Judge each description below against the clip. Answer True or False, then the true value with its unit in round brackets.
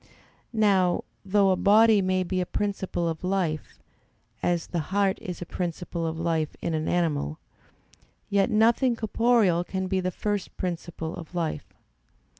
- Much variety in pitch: False (2.9 semitones)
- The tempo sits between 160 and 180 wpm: False (150 wpm)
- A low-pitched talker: False (185 Hz)